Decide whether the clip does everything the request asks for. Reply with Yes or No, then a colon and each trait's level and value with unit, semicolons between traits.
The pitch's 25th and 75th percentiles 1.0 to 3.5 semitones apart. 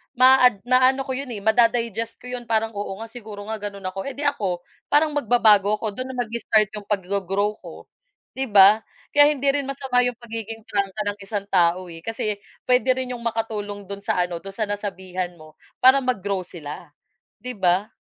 No: average, 4.1 semitones